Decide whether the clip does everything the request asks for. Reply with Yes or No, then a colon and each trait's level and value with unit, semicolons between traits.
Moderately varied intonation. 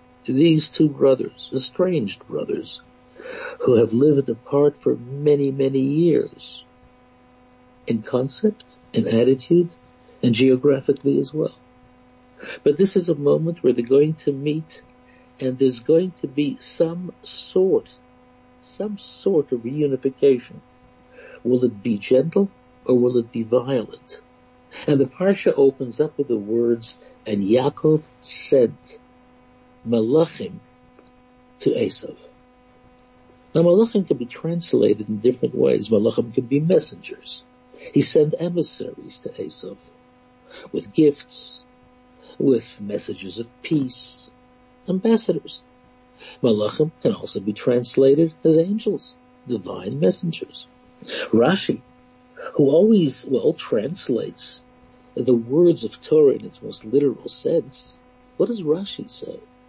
No: wide, 8.4 semitones